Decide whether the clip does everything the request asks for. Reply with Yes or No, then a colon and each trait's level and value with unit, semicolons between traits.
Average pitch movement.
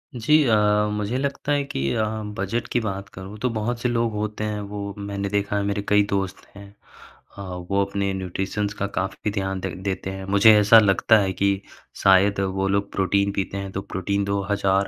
No: narrow, 1.6 semitones